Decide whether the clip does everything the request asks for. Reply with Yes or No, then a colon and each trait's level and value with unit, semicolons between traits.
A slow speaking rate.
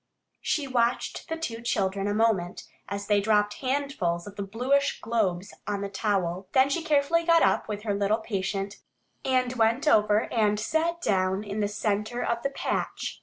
No: average, 175 wpm